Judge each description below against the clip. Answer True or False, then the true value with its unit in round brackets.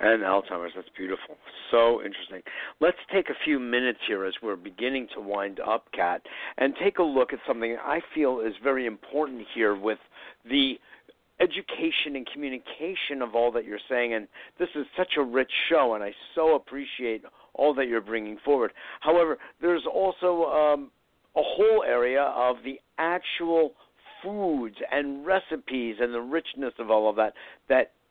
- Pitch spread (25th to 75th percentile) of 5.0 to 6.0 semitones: True (5.6 semitones)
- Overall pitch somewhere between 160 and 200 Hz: False (130 Hz)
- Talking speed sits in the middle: True (165 wpm)